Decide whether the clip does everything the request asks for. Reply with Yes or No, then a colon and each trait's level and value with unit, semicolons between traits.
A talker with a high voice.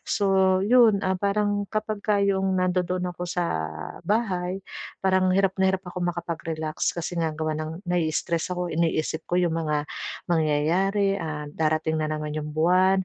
No: medium, 180 Hz